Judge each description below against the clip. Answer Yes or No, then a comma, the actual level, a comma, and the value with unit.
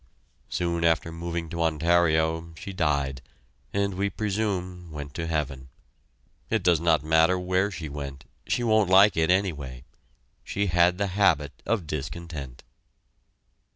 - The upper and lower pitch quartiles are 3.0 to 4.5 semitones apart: Yes, average, 3.3 semitones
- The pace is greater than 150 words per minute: No, slow, 135 wpm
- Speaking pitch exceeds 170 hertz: No, very low, 85 Hz